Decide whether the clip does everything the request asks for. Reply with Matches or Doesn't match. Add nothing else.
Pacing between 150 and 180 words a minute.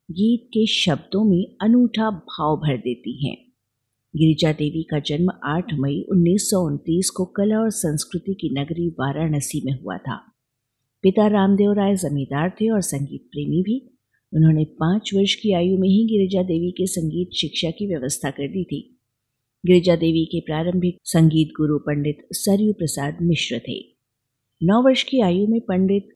Matches